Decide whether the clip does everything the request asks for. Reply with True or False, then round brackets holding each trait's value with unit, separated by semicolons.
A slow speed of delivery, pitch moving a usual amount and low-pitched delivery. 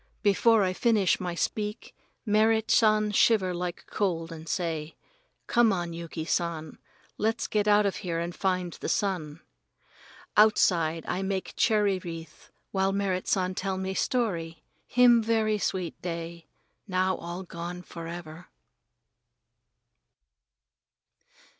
False (120 wpm; 3.7 semitones; 185 Hz)